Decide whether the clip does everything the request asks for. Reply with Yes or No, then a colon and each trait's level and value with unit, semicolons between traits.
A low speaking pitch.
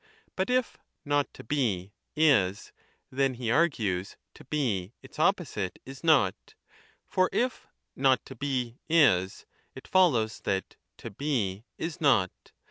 Yes: low, 130 Hz